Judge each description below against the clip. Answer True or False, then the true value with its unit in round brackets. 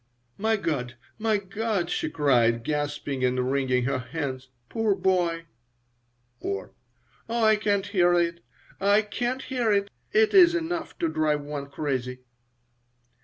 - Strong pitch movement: True (7.6 semitones)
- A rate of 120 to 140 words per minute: True (135 wpm)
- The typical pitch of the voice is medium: True (170 Hz)